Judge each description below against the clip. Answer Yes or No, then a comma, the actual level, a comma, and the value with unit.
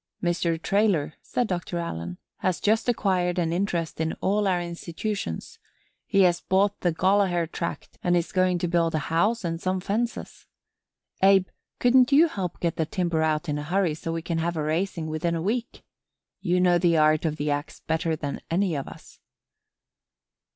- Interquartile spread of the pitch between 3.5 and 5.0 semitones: No, average, 3.0 semitones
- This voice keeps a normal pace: Yes, average, 180 wpm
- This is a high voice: No, medium, 175 Hz